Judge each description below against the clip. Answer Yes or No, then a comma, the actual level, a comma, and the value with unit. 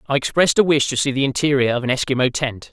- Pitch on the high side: No, low, 135 Hz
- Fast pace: Yes, fast, 265 wpm